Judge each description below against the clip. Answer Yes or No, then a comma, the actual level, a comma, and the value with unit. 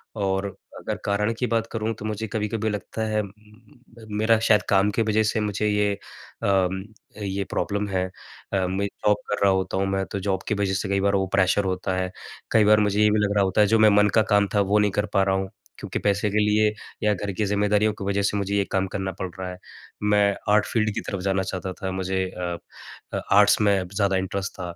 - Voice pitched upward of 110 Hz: No, low, 100 Hz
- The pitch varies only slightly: Yes, narrow, 1.5 semitones